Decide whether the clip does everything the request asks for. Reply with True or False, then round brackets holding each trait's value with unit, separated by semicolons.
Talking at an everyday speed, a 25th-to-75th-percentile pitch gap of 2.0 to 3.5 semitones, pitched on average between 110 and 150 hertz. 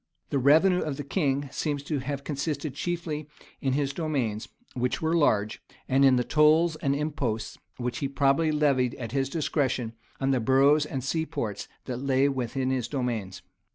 True (165 wpm; 3.0 semitones; 140 Hz)